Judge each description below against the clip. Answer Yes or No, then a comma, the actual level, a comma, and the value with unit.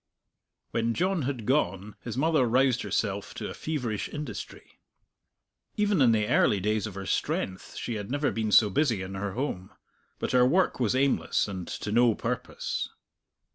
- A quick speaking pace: No, average, 170 wpm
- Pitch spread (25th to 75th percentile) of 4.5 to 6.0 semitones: Yes, average, 4.9 semitones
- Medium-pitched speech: No, low, 115 Hz